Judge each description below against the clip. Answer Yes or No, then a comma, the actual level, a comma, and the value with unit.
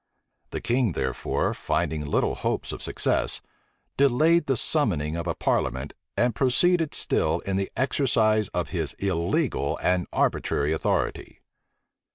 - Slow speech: Yes, slow, 130 wpm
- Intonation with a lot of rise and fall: Yes, wide, 8.5 semitones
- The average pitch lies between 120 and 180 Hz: No, low, 100 Hz